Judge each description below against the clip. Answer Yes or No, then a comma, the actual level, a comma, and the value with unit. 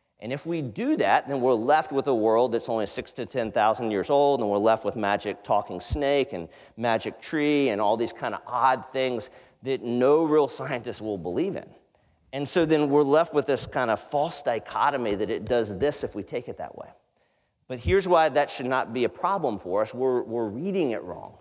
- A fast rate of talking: Yes, fast, 220 wpm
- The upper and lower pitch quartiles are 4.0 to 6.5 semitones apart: Yes, average, 4.4 semitones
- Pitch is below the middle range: Yes, low, 130 Hz